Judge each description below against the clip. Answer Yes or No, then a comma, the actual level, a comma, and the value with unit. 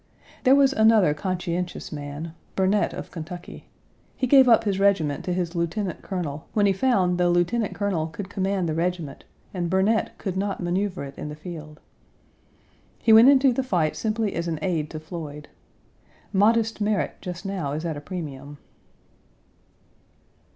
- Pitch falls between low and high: Yes, medium, 180 Hz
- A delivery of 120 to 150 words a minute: No, average, 160 wpm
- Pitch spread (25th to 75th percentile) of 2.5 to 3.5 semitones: No, average, 4.2 semitones